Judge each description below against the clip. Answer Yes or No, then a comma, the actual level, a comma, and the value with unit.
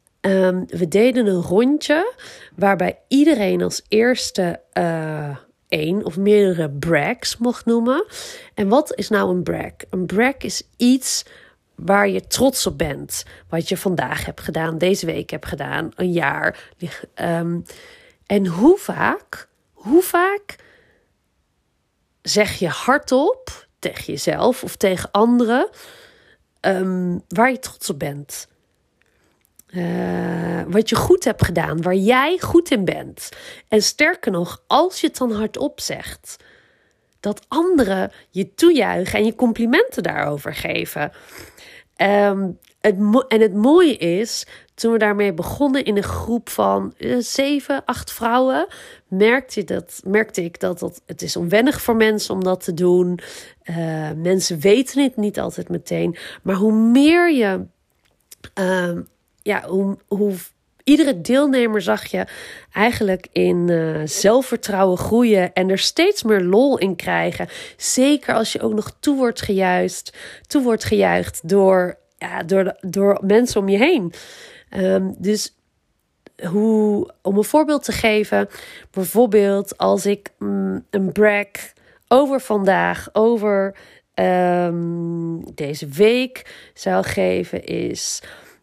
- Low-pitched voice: No, high, 205 Hz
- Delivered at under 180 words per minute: Yes, slow, 135 wpm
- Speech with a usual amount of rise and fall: No, wide, 5.9 semitones